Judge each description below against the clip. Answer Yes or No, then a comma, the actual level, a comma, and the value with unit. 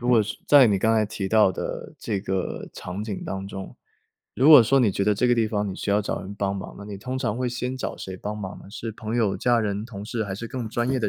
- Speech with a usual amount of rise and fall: Yes, average, 3.2 semitones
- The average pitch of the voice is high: No, low, 110 Hz